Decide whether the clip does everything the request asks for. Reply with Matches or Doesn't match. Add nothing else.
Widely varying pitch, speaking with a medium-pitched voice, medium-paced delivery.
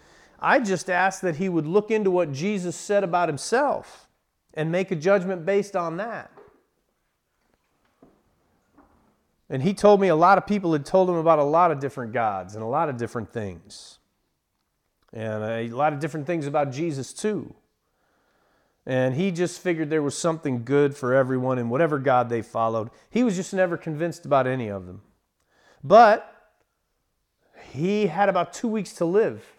Matches